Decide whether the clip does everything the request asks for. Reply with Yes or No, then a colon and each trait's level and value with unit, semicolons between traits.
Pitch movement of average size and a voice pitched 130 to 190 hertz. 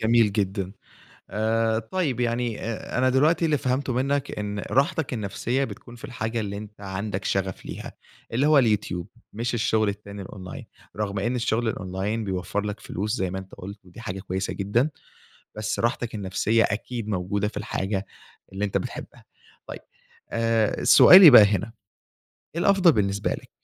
No: average, 3.4 semitones; low, 110 Hz